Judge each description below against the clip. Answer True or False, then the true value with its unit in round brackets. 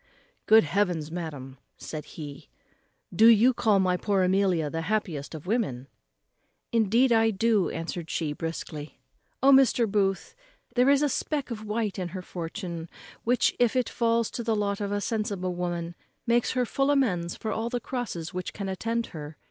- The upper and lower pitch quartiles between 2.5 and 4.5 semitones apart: False (5.4 semitones)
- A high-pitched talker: True (200 Hz)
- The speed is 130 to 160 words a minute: False (170 wpm)